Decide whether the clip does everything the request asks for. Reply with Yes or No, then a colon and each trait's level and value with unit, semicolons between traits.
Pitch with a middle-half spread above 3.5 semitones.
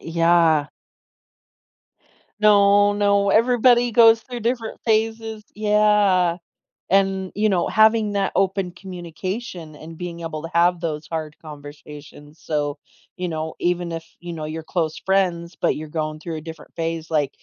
Yes: average, 4.4 semitones